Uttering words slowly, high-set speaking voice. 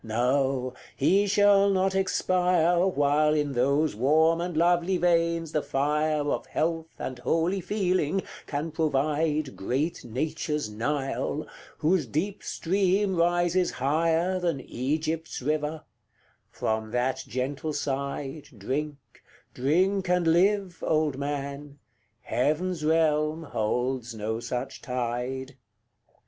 No: slow, 110 wpm; medium, 155 Hz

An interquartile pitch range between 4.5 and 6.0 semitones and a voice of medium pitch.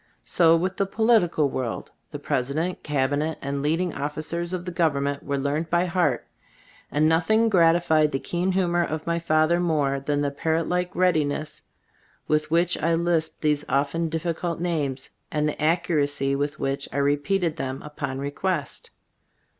No: average, 3.3 semitones; medium, 155 Hz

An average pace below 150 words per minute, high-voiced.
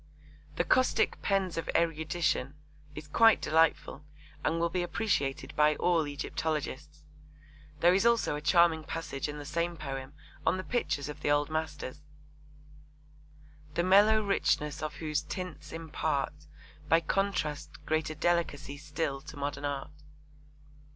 No: slow, 135 wpm; medium, 155 Hz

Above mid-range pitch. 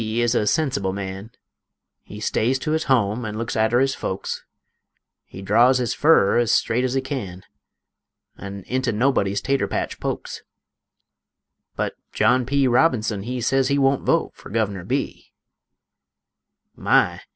No: low, 120 Hz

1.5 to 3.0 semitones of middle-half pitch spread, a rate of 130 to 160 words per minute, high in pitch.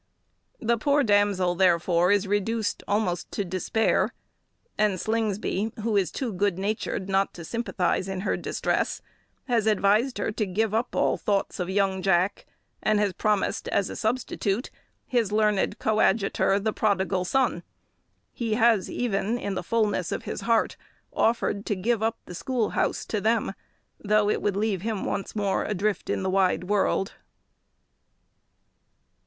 Yes: narrow, 2.5 semitones; average, 155 wpm; high, 205 Hz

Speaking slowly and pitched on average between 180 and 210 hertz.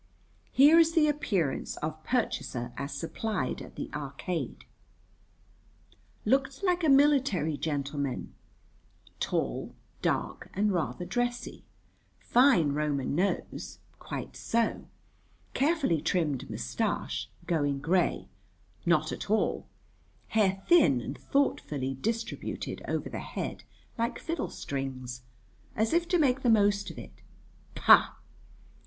Yes: slow, 110 wpm; high, 190 Hz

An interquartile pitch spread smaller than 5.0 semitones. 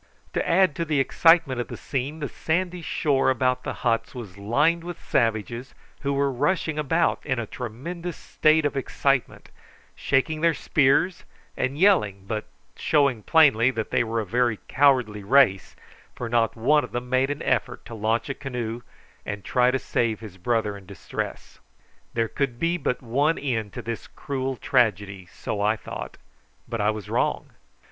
Yes: average, 4.5 semitones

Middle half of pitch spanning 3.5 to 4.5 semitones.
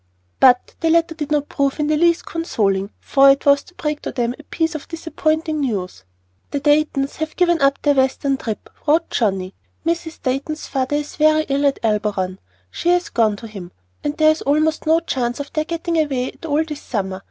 Yes: average, 4.0 semitones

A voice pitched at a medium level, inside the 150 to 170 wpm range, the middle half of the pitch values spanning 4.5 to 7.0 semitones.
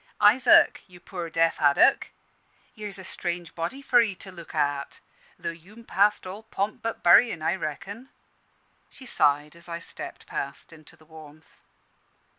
Yes: medium, 175 Hz; average, 155 wpm; average, 4.8 semitones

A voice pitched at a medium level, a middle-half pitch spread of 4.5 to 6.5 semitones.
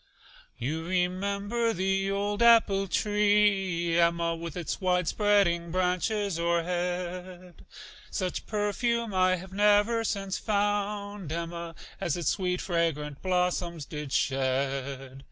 No: medium, 180 Hz; average, 3.2 semitones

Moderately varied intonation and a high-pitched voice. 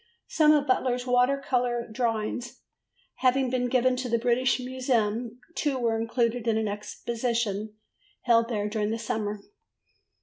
No: narrow, 2.2 semitones; high, 240 Hz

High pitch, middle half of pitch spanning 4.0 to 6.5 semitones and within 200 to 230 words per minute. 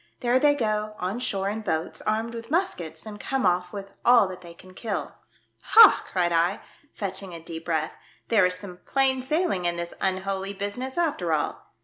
Yes: high, 195 Hz; average, 5.0 semitones; fast, 205 wpm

